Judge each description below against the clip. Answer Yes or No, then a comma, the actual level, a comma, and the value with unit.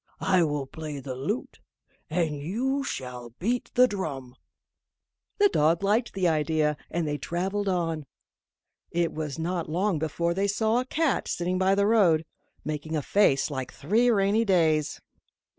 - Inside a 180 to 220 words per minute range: No, average, 155 wpm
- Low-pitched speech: No, medium, 170 Hz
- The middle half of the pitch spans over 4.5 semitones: Yes, average, 5.1 semitones